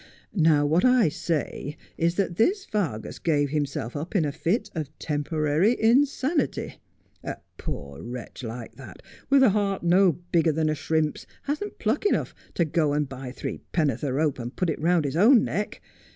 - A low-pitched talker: No, medium, 160 Hz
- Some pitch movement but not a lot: No, wide, 6.0 semitones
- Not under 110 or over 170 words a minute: No, average, 180 wpm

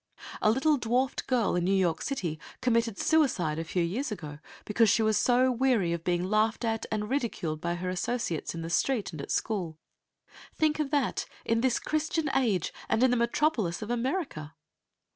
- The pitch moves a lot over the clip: Yes, wide, 6.6 semitones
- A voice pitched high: Yes, high, 225 Hz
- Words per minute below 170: No, average, 185 wpm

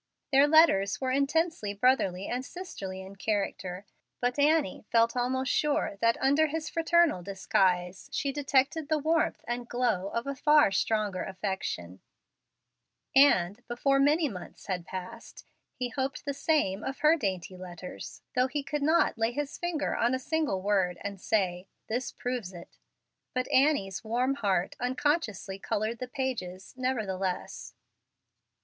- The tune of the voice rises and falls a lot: Yes, wide, 6.6 semitones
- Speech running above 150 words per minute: No, average, 145 wpm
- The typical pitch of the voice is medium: No, high, 245 Hz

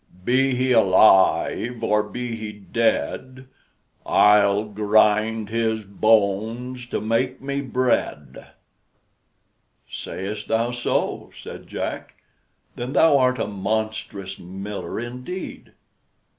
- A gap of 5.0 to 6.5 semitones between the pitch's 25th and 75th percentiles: No, average, 3.1 semitones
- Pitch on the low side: Yes, low, 110 Hz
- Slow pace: Yes, slow, 100 wpm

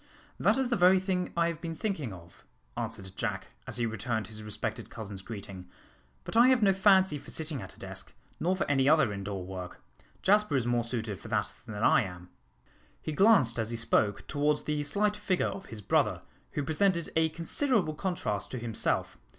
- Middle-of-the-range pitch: Yes, medium, 145 Hz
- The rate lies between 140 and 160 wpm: No, average, 195 wpm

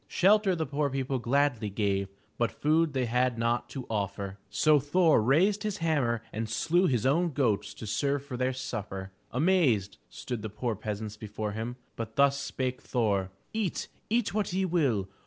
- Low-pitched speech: Yes, low, 130 Hz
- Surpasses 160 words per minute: Yes, average, 175 wpm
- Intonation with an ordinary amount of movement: No, wide, 6.0 semitones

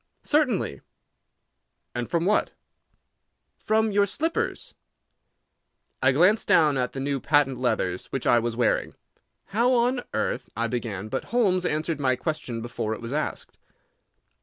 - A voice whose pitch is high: No, medium, 145 Hz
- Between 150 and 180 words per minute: No, slow, 135 wpm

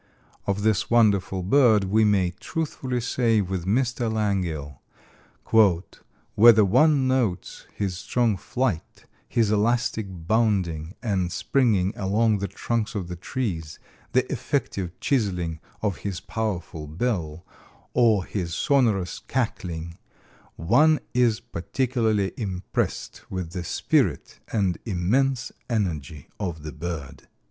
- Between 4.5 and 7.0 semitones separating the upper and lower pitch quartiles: Yes, average, 4.9 semitones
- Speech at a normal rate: No, slow, 115 wpm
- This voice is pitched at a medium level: No, low, 100 Hz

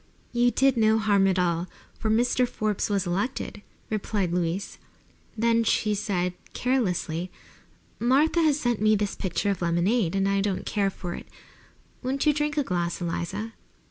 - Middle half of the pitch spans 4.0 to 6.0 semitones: Yes, average, 4.8 semitones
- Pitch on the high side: Yes, high, 205 Hz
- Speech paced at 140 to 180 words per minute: Yes, average, 160 wpm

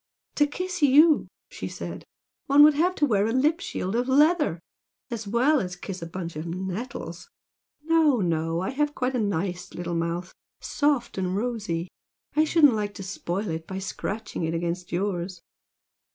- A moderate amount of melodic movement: No, wide, 8.5 semitones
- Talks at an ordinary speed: Yes, average, 165 wpm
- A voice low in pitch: No, high, 205 Hz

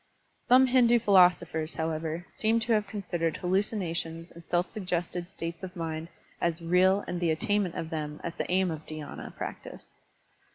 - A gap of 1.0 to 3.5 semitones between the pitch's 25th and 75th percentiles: Yes, average, 3.0 semitones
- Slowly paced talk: No, average, 160 wpm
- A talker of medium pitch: Yes, medium, 175 Hz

